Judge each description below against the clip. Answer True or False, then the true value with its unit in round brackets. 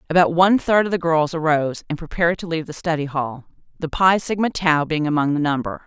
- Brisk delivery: True (225 wpm)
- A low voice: False (160 Hz)